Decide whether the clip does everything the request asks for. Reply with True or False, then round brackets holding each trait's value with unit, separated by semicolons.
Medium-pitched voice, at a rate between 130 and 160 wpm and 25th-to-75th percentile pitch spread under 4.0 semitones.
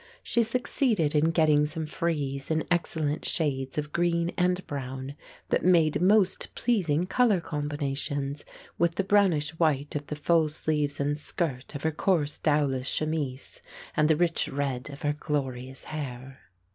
True (150 Hz; 150 wpm; 3.1 semitones)